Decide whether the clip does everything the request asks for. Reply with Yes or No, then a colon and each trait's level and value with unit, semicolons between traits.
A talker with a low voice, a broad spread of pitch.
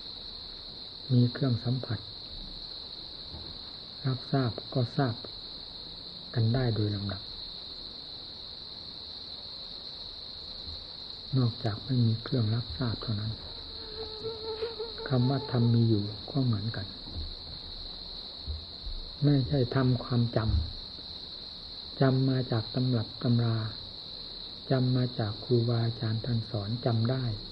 Yes: low, 110 Hz; wide, 6.0 semitones